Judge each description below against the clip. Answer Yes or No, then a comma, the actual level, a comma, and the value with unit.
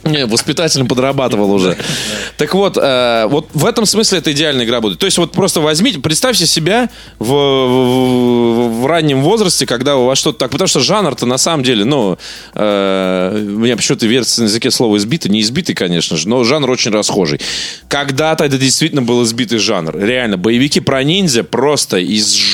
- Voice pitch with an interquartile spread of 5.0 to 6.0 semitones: Yes, average, 5.3 semitones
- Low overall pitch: Yes, low, 130 Hz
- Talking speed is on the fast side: Yes, fast, 180 wpm